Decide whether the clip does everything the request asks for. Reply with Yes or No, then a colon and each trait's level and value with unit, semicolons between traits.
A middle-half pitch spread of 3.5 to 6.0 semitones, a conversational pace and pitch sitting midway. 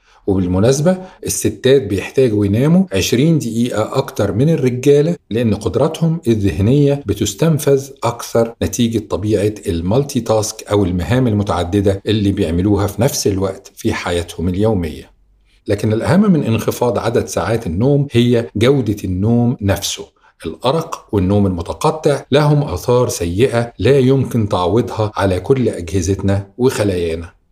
No: average, 5.2 semitones; average, 115 wpm; low, 110 Hz